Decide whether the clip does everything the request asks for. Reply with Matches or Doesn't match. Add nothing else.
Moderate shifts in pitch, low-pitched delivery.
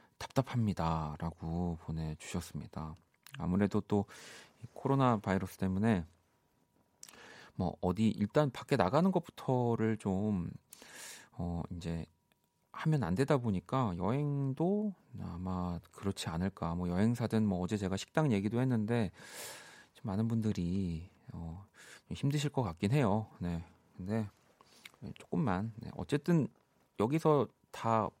Doesn't match